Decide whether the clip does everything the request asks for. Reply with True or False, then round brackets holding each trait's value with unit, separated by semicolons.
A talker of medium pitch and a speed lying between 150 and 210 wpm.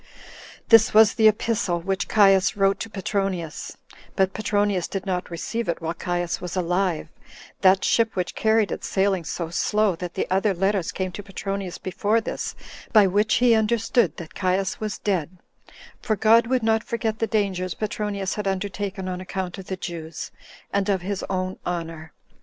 False (195 Hz; 170 wpm)